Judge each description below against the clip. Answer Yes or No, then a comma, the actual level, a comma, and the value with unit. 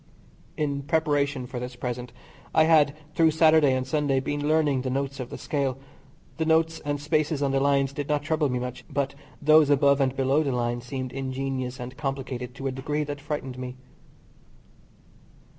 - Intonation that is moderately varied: No, narrow, 2.2 semitones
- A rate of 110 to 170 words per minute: No, average, 180 wpm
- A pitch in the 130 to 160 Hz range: Yes, medium, 140 Hz